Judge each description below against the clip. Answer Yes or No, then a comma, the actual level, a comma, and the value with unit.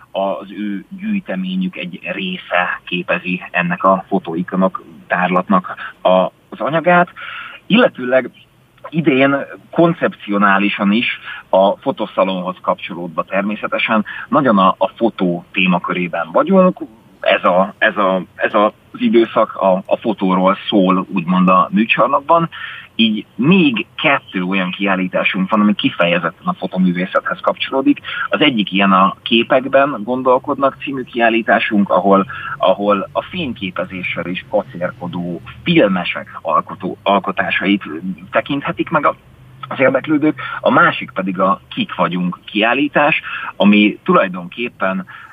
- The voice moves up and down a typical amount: No, wide, 6.8 semitones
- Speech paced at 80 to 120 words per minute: Yes, slow, 105 wpm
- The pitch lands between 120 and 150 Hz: No, low, 105 Hz